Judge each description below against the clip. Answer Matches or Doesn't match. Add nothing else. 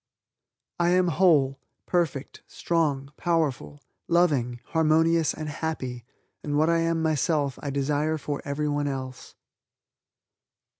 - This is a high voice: Doesn't match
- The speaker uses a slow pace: Matches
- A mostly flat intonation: Doesn't match